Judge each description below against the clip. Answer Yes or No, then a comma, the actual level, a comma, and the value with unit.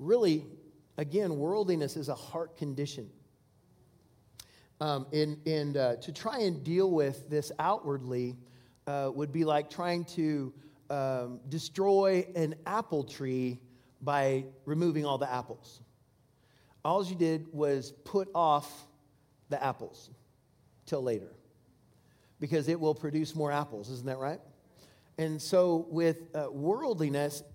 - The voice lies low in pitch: No, medium, 145 Hz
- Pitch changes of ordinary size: Yes, average, 3.2 semitones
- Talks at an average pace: No, slow, 125 wpm